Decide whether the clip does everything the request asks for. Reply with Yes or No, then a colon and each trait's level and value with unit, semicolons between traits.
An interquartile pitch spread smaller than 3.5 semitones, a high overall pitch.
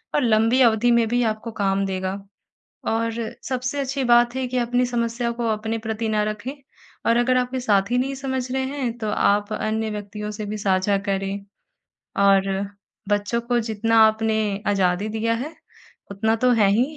Yes: average, 2.9 semitones; high, 225 Hz